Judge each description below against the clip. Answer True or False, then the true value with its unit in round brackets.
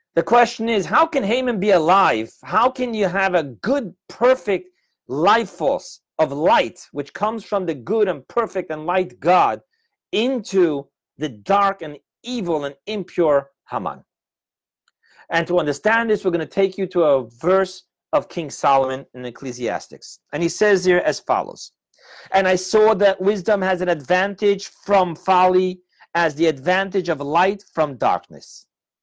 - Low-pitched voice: False (185 Hz)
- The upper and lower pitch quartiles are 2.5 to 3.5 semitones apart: False (4.0 semitones)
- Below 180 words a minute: True (160 wpm)